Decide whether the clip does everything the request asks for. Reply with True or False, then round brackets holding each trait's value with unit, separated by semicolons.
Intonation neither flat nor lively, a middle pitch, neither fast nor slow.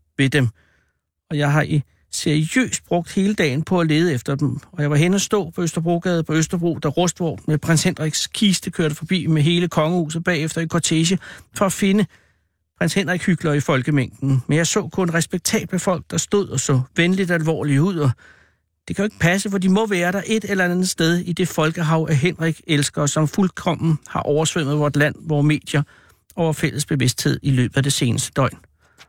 True (3.6 semitones; 160 Hz; 200 wpm)